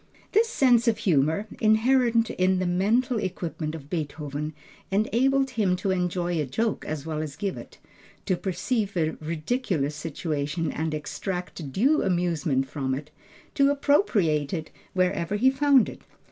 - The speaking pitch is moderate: Yes, medium, 180 Hz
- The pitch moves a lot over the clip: Yes, wide, 6.7 semitones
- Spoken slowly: No, average, 145 wpm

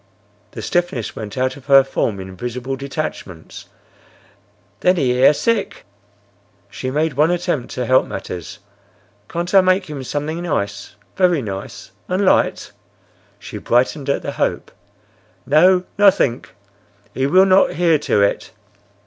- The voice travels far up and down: Yes, wide, 6.0 semitones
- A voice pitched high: No, medium, 140 Hz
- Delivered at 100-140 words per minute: Yes, slow, 135 wpm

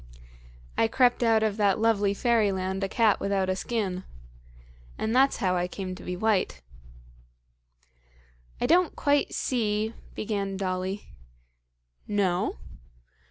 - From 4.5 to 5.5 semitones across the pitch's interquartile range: No, average, 3.0 semitones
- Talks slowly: Yes, slow, 125 wpm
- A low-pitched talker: No, high, 205 Hz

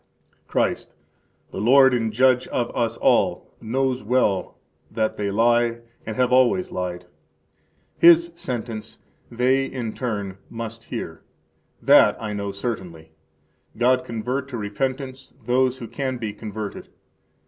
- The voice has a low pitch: Yes, low, 120 Hz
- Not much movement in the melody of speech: No, average, 3.2 semitones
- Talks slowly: Yes, slow, 125 wpm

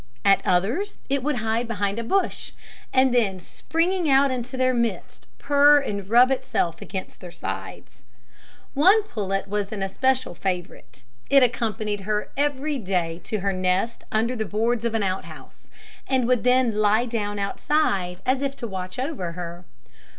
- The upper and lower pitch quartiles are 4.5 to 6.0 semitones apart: Yes, average, 5.1 semitones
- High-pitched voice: Yes, high, 225 Hz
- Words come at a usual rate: Yes, average, 165 wpm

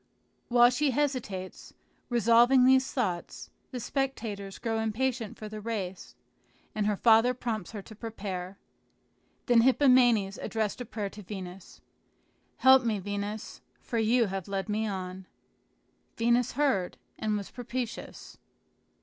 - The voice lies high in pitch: Yes, high, 220 Hz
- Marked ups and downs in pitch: No, average, 3.6 semitones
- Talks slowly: Yes, slow, 130 wpm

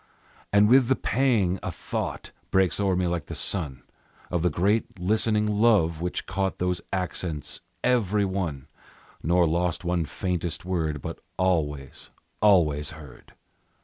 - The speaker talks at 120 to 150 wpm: Yes, average, 140 wpm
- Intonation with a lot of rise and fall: No, average, 3.6 semitones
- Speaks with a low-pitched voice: Yes, very low, 90 Hz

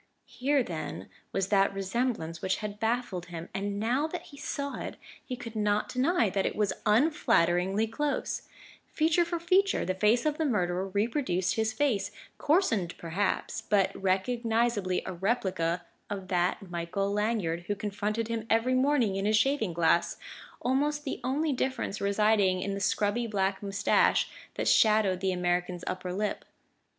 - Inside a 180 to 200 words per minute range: No, average, 155 wpm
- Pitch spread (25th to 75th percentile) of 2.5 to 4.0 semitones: No, average, 4.8 semitones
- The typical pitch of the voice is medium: No, high, 210 Hz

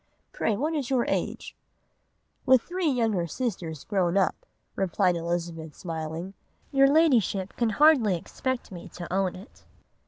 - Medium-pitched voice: No, high, 195 Hz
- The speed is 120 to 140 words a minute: Yes, slow, 135 wpm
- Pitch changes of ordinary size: No, wide, 7.0 semitones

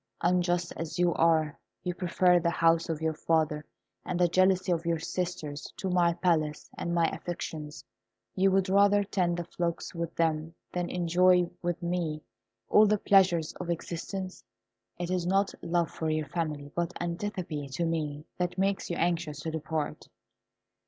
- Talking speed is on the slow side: No, average, 165 wpm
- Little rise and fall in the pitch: Yes, narrow, 2.1 semitones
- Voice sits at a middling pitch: Yes, medium, 170 Hz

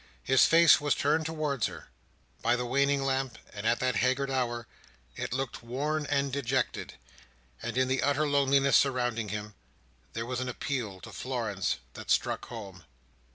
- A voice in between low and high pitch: No, low, 130 Hz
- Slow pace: No, average, 160 wpm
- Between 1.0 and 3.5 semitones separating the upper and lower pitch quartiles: Yes, average, 2.9 semitones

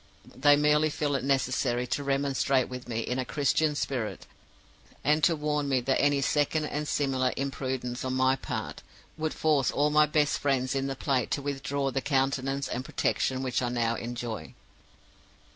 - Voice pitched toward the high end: No, low, 135 Hz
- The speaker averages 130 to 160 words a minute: No, average, 175 wpm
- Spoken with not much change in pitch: Yes, narrow, 2.2 semitones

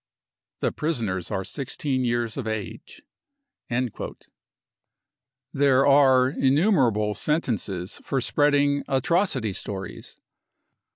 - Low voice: Yes, low, 130 Hz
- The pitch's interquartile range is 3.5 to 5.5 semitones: Yes, average, 4.6 semitones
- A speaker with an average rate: No, slow, 100 wpm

